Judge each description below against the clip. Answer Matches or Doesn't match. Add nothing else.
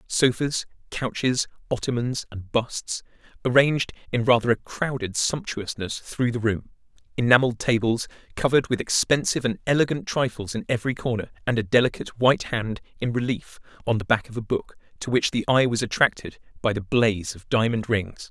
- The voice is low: Matches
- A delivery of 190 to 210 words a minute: Doesn't match